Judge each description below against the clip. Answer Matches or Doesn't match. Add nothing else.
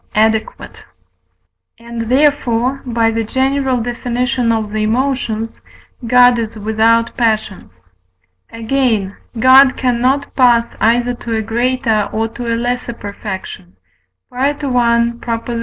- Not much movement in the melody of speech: Matches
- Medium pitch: Doesn't match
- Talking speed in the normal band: Doesn't match